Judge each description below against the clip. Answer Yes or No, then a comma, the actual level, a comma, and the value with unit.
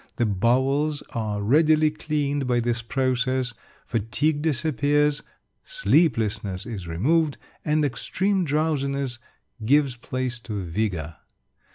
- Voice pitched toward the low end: Yes, low, 130 Hz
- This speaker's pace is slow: Yes, slow, 100 wpm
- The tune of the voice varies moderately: Yes, average, 4.8 semitones